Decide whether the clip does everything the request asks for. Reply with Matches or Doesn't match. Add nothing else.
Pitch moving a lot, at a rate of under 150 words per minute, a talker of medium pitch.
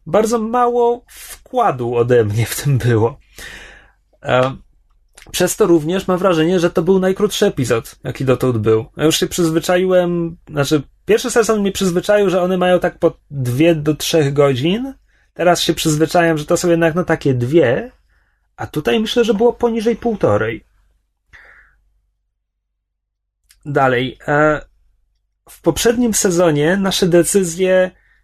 Matches